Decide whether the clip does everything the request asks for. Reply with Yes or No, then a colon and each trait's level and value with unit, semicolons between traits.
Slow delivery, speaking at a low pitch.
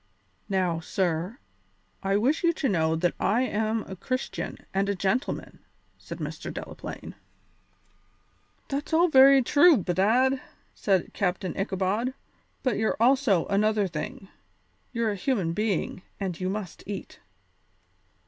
No: slow, 130 wpm; high, 205 Hz